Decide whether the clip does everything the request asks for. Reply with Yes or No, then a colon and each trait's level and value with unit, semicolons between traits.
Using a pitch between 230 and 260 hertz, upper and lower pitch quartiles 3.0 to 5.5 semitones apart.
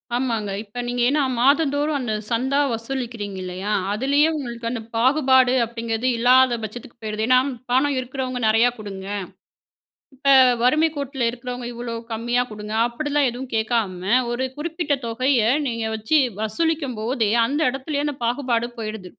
Yes: high, 245 Hz; average, 3.3 semitones